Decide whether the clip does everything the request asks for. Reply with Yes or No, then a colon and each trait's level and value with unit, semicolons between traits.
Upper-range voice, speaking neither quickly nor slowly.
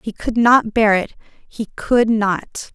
Yes: high, 220 Hz; average, 155 wpm